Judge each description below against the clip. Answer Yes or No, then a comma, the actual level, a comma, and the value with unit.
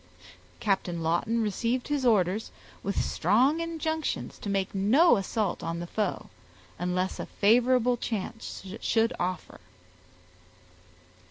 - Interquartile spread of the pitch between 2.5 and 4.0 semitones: No, average, 5.0 semitones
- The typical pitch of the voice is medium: No, high, 215 Hz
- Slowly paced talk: Yes, slow, 110 wpm